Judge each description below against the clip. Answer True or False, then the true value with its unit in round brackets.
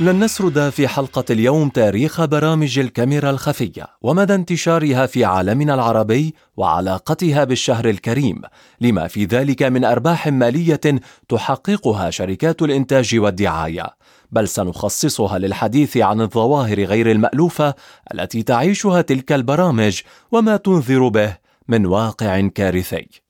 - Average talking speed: True (115 wpm)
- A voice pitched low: True (130 Hz)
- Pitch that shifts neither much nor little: False (5.7 semitones)